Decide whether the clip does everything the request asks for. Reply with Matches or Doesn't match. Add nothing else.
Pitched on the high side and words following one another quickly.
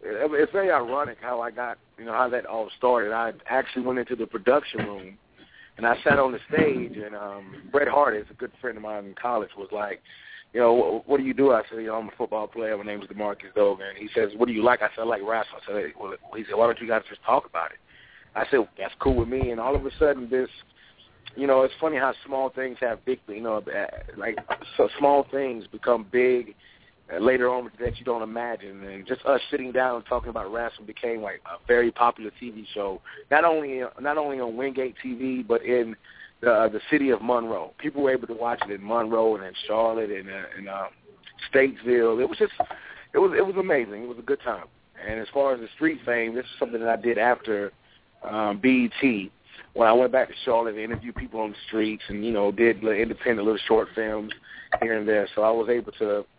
Doesn't match